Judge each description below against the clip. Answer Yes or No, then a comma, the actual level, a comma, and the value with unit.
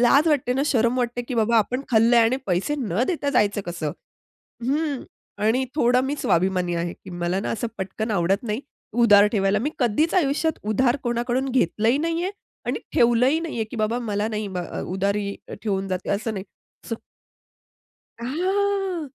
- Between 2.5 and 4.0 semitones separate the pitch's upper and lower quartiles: No, average, 4.9 semitones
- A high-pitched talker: Yes, high, 235 Hz